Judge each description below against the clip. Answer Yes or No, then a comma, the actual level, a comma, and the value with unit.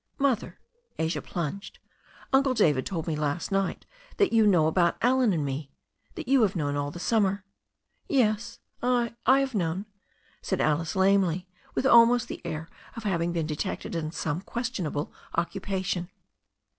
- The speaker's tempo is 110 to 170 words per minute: Yes, average, 165 wpm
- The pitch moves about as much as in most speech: No, wide, 6.2 semitones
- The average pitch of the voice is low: No, high, 190 Hz